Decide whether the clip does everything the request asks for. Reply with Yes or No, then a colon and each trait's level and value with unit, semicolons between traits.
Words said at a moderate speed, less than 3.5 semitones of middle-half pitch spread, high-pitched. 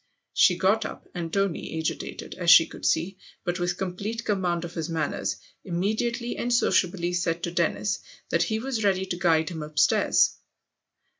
No: average, 170 wpm; average, 2.8 semitones; medium, 180 Hz